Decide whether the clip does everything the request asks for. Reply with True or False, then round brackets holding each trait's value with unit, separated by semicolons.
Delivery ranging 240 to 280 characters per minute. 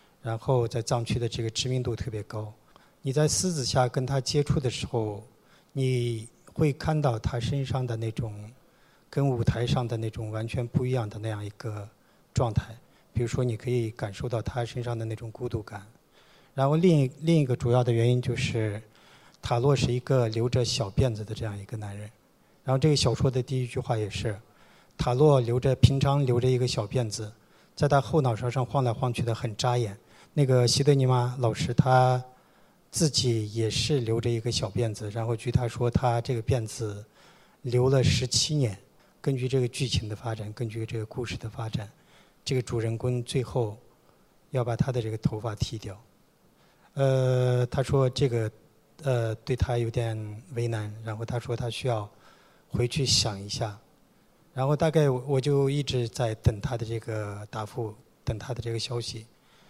True (260 characters per minute)